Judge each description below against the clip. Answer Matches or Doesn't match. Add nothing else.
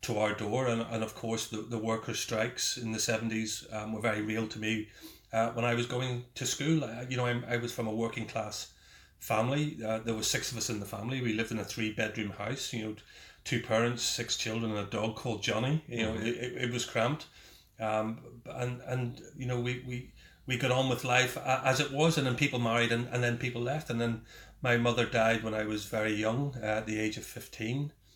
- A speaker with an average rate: Doesn't match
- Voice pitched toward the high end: Doesn't match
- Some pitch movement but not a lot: Doesn't match